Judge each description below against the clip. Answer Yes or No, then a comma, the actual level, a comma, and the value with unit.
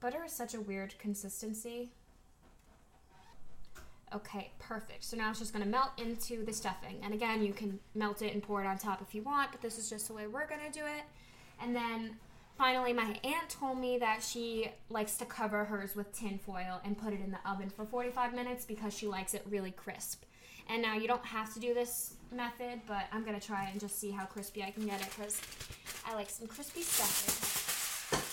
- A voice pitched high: Yes, high, 215 Hz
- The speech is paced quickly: Yes, fast, 210 wpm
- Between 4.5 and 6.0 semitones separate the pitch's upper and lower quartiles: No, average, 2.9 semitones